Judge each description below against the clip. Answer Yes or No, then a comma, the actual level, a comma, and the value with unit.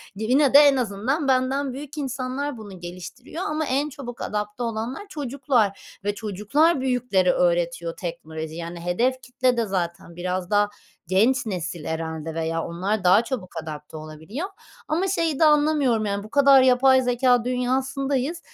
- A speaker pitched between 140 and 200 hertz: No, high, 240 Hz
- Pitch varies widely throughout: Yes, wide, 6.9 semitones